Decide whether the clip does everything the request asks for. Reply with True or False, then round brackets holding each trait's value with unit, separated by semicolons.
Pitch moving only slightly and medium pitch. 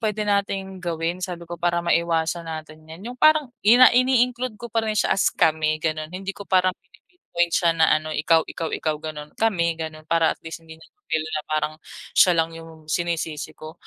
False (3.7 semitones; 170 Hz)